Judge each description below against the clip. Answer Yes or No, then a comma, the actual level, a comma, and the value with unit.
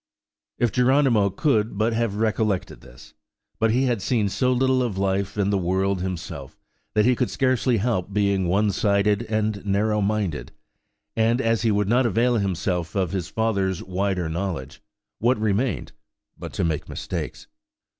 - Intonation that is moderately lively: Yes, average, 3.1 semitones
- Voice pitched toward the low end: Yes, low, 105 Hz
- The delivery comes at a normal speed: Yes, average, 160 wpm